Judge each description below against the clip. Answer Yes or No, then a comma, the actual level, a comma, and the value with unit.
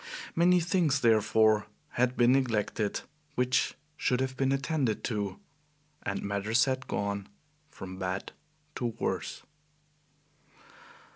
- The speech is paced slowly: Yes, slow, 110 wpm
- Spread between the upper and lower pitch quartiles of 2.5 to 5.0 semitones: Yes, average, 4.6 semitones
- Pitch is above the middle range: No, low, 120 Hz